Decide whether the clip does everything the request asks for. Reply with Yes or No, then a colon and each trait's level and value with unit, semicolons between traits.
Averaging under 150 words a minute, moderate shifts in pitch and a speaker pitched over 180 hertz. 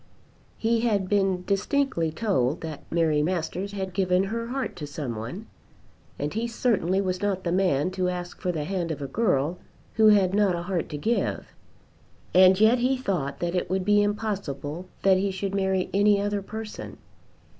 No: average, 180 wpm; average, 3.2 semitones; high, 190 Hz